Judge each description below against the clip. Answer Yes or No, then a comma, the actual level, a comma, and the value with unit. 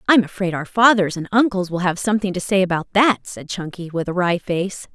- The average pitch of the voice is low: No, high, 190 Hz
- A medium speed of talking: No, fast, 245 wpm